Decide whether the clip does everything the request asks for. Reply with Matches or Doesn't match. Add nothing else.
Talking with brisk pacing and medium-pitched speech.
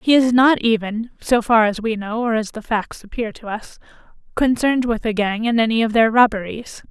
Doesn't match